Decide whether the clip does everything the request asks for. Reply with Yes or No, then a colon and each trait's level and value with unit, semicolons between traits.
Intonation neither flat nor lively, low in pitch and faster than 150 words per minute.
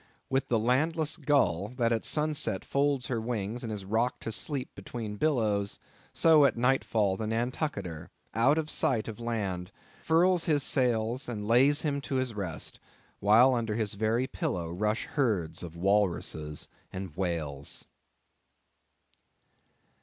No: average, 4.9 semitones; low, 115 Hz; average, 140 wpm